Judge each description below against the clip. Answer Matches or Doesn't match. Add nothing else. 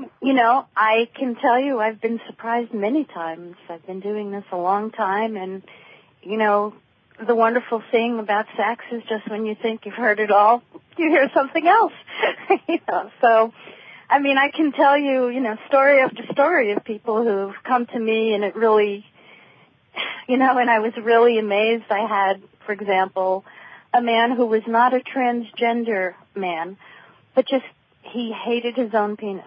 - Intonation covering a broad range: Doesn't match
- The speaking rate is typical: Matches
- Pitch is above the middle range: Matches